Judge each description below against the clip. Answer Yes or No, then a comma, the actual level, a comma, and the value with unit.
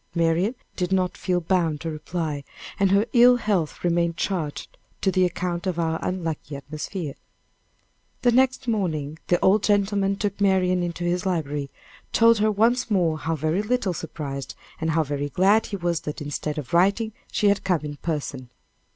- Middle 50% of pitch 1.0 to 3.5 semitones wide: No, average, 4.2 semitones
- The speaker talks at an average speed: Yes, average, 170 wpm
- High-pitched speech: No, medium, 175 Hz